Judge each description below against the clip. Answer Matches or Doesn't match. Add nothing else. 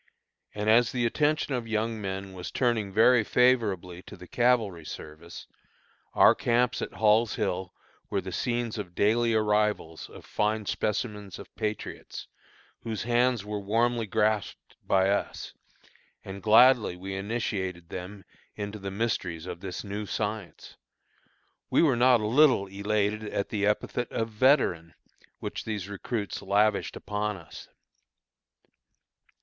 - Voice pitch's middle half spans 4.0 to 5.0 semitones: Doesn't match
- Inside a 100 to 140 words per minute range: Matches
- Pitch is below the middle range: Matches